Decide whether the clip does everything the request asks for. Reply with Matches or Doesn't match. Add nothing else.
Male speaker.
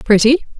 Doesn't match